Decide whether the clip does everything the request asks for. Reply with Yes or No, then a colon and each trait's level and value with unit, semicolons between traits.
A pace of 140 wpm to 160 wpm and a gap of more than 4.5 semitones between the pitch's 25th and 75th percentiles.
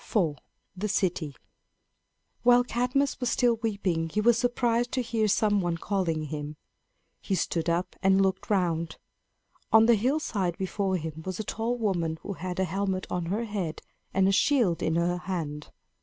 No: average, 170 wpm; average, 4.9 semitones